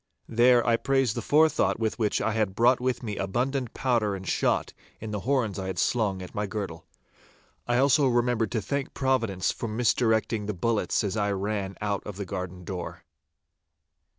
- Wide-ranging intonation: No, average, 3.7 semitones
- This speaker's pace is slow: No, average, 180 wpm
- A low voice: Yes, low, 110 Hz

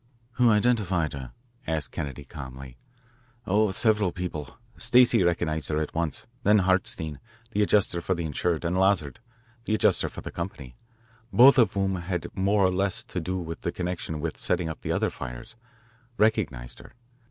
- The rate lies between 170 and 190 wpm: Yes, average, 175 wpm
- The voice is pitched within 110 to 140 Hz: No, very low, 90 Hz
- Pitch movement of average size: Yes, average, 4.4 semitones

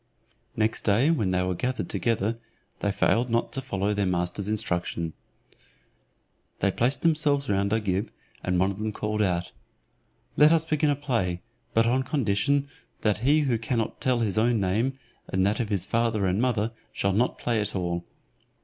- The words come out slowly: No, average, 175 wpm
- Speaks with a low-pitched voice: Yes, low, 110 Hz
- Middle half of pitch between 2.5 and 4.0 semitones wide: No, average, 4.5 semitones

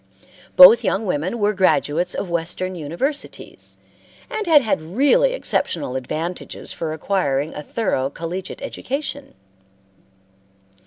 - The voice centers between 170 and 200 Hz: Yes, medium, 185 Hz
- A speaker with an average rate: No, slow, 110 wpm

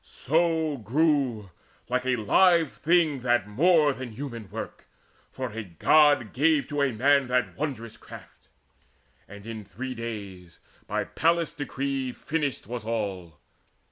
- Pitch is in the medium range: No, low, 130 Hz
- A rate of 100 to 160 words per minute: Yes, slow, 135 wpm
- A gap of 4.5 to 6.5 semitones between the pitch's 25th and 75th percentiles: Yes, average, 5.1 semitones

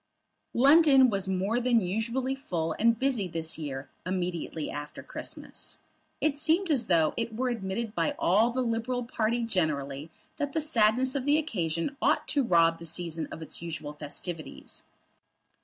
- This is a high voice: Yes, high, 220 Hz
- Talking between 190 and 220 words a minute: No, average, 155 wpm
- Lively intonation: Yes, wide, 7.5 semitones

